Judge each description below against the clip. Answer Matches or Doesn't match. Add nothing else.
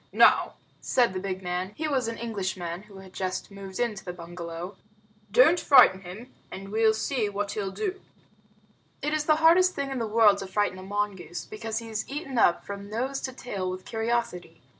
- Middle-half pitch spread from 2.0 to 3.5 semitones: Doesn't match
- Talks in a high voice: Matches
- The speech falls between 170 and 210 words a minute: Matches